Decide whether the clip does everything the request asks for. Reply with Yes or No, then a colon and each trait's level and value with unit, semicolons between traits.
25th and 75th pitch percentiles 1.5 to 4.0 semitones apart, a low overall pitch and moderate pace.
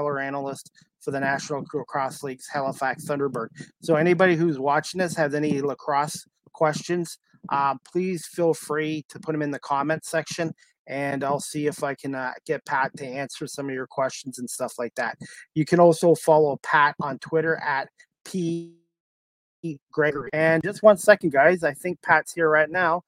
No: average, 3.2 semitones; medium, 150 Hz; average, 175 wpm